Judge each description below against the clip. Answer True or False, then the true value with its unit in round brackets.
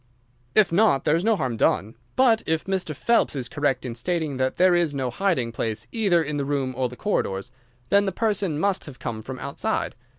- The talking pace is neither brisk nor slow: False (210 wpm)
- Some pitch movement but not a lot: False (6.9 semitones)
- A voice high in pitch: False (150 Hz)